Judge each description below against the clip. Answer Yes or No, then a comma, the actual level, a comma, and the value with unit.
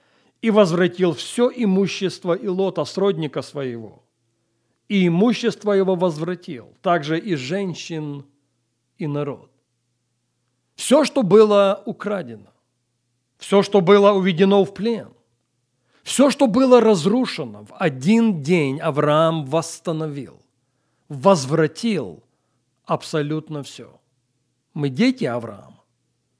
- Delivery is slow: Yes, slow, 95 wpm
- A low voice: No, medium, 165 Hz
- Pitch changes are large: Yes, wide, 7.8 semitones